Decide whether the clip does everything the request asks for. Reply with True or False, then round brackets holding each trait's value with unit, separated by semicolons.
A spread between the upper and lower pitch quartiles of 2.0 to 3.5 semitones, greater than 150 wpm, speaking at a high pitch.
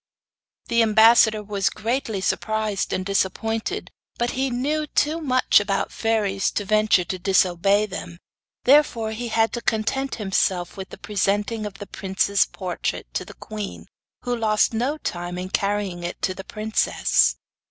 False (3.0 semitones; 145 wpm; 215 Hz)